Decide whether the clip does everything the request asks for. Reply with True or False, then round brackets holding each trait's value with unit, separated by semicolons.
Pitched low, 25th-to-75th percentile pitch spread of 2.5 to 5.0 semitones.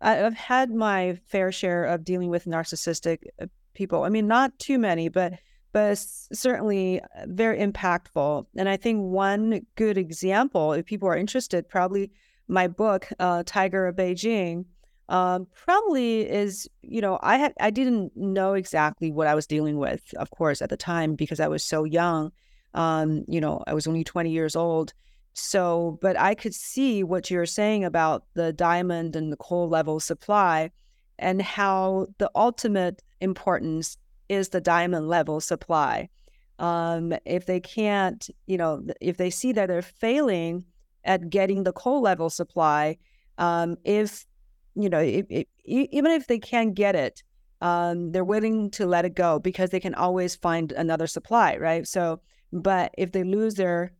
False (185 Hz; 3.4 semitones)